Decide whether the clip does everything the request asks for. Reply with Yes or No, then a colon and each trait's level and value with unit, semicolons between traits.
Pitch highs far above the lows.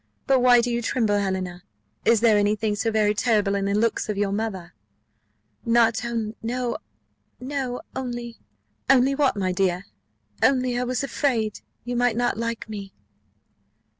No: average, 3.2 semitones